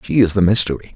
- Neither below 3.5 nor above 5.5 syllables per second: No, 7.1 syllables/s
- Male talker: Yes, male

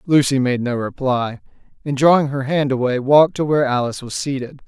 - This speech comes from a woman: No, male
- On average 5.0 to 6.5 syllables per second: Yes, 5.9 syllables/s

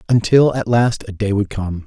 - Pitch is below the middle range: Yes, low, 110 Hz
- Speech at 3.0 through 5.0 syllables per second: Yes, 4.9 syllables/s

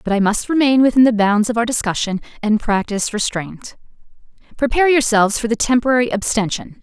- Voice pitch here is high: Yes, high, 230 Hz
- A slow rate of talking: No, average, 165 wpm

